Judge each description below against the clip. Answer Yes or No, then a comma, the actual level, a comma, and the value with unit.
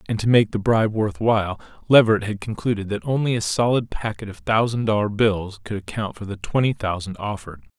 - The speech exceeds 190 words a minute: Yes, average, 200 wpm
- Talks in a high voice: No, low, 105 Hz